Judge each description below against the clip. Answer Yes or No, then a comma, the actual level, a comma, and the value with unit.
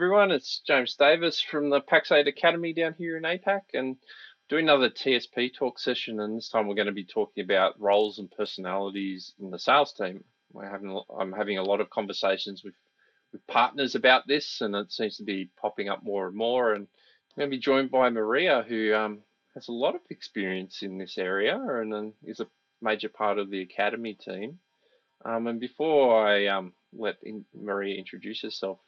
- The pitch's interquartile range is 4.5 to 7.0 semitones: Yes, average, 5.2 semitones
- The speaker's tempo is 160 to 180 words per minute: No, average, 195 wpm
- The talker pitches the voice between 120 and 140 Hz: No, low, 110 Hz